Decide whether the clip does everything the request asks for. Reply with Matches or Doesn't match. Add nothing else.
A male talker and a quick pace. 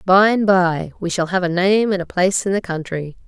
Doesn't match